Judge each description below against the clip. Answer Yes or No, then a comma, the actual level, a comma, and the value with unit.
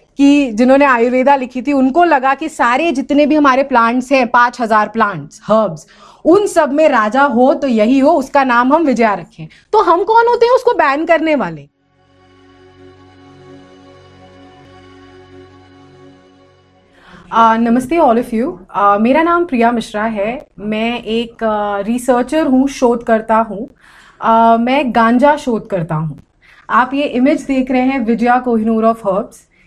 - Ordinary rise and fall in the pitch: No, wide, 6.1 semitones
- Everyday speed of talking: Yes, average, 150 wpm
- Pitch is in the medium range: No, high, 235 Hz